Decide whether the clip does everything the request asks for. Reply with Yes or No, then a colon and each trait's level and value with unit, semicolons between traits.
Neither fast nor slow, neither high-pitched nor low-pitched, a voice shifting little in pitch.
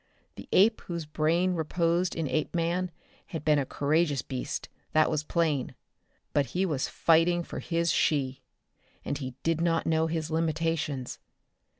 Yes: average, 150 wpm; medium, 160 Hz; narrow, 2.2 semitones